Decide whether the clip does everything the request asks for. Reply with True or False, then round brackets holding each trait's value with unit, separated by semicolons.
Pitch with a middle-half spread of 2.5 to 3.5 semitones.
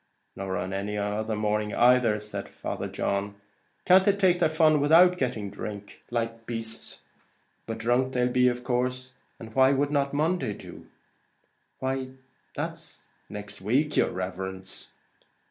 False (4.5 semitones)